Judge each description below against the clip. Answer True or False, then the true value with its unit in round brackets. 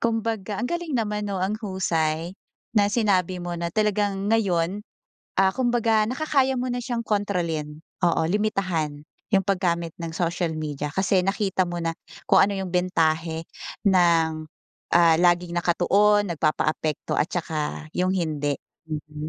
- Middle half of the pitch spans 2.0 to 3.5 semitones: False (4.1 semitones)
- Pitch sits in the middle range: True (180 Hz)